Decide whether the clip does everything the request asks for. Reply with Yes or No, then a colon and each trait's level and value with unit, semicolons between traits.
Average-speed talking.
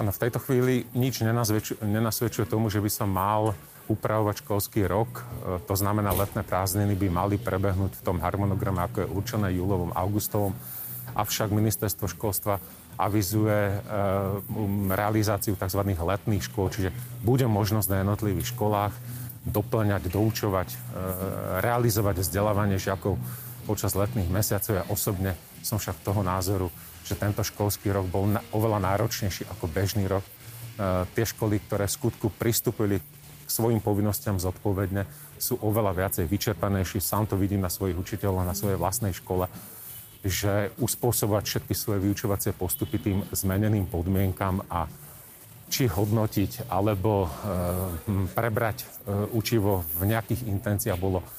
Yes: average, 135 wpm